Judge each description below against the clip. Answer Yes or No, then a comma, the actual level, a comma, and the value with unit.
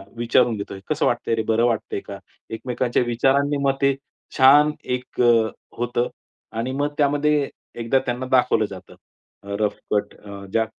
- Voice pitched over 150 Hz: No, low, 120 Hz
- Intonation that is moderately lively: Yes, average, 3.3 semitones